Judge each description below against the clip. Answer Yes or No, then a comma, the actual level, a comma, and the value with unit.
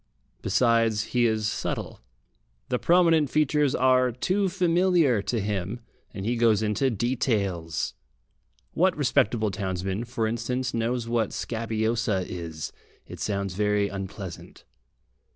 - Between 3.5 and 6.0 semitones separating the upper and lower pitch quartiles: Yes, average, 3.9 semitones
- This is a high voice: No, low, 115 Hz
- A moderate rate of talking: No, slow, 115 wpm